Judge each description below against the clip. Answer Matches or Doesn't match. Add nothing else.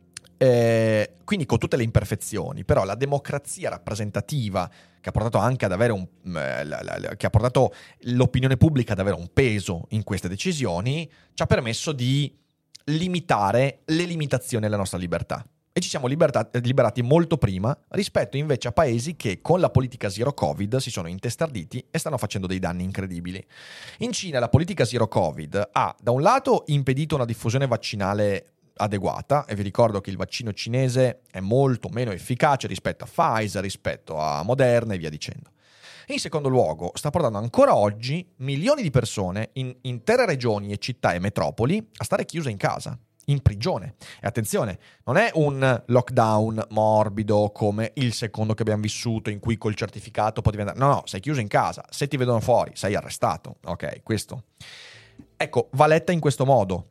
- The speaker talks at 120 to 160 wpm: Doesn't match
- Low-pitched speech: Matches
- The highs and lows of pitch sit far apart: Doesn't match